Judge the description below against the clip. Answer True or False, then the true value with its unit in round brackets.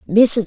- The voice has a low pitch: False (185 Hz)